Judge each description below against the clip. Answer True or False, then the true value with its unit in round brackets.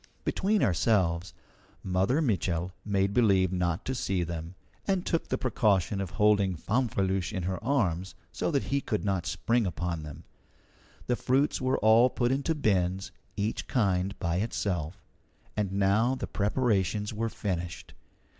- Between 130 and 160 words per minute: True (145 wpm)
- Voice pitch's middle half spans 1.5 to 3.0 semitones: False (4.5 semitones)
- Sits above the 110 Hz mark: False (100 Hz)